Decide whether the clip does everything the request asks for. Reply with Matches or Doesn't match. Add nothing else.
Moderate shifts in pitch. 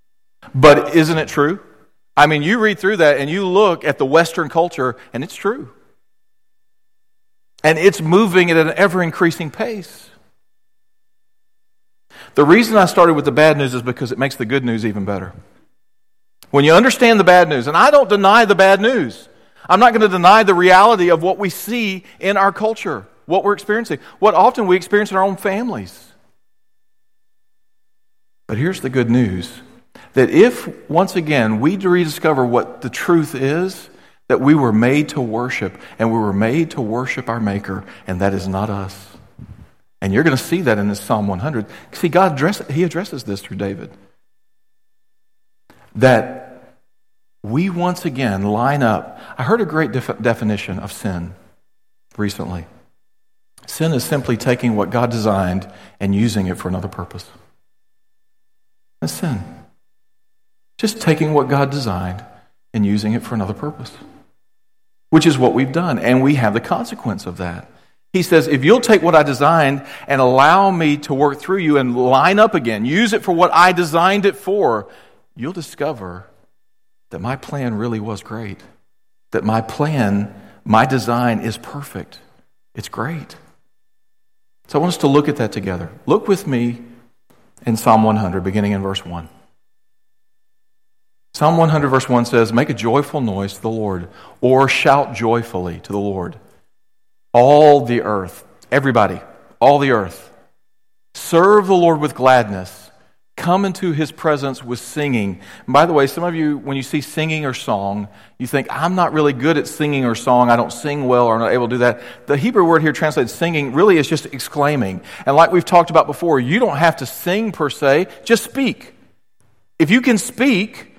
Doesn't match